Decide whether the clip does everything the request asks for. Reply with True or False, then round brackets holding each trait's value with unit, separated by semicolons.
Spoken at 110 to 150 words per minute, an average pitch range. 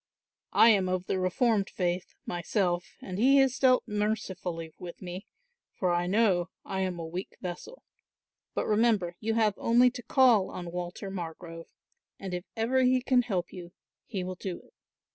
False (170 wpm; 4.4 semitones)